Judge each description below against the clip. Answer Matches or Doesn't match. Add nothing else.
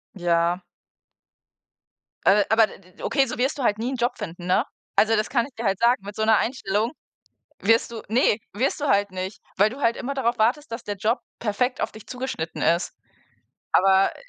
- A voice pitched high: Matches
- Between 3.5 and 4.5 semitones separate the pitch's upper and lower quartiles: Matches